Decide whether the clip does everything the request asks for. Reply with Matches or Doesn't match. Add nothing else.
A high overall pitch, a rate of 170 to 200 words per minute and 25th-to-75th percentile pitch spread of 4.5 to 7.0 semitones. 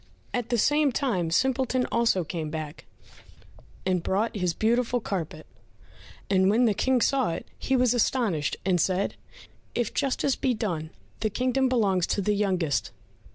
Doesn't match